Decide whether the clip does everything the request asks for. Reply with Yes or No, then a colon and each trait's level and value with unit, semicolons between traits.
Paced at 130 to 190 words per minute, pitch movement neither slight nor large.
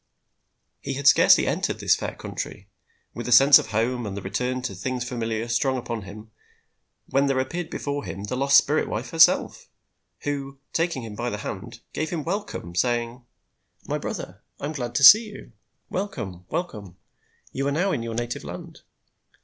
Yes: average, 180 wpm; average, 4.1 semitones